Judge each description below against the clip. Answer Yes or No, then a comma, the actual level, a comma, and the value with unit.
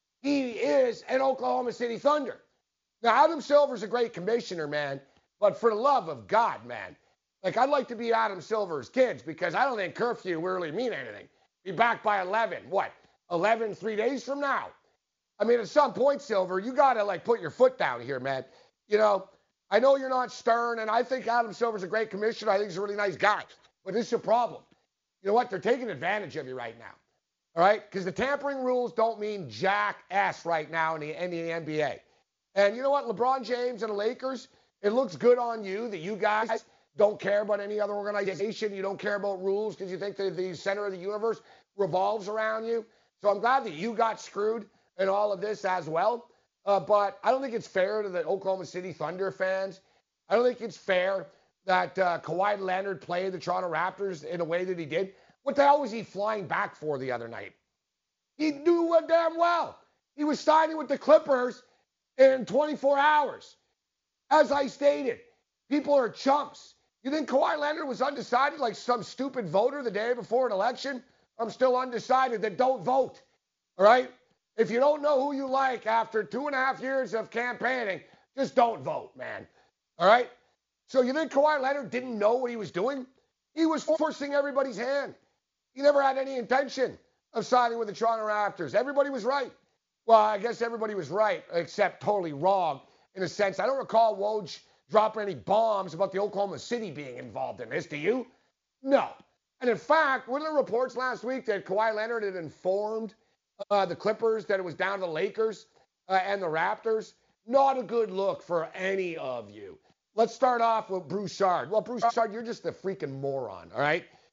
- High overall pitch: Yes, high, 225 Hz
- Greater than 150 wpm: Yes, average, 200 wpm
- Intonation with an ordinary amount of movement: Yes, average, 4.9 semitones